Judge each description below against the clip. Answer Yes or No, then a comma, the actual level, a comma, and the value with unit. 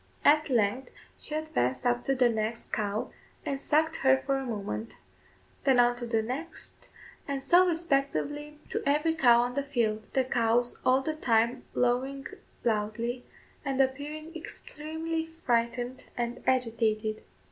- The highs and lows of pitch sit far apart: No, average, 3.9 semitones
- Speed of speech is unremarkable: Yes, average, 145 wpm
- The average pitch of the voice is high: Yes, very high, 255 Hz